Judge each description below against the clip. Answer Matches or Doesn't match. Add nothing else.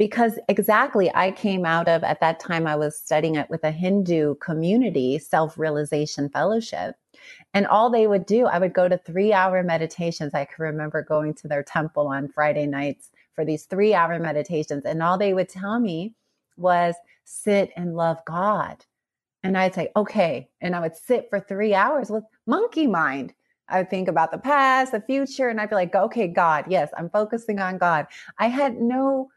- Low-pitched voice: Doesn't match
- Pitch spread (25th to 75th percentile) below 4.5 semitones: Doesn't match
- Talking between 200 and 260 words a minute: Doesn't match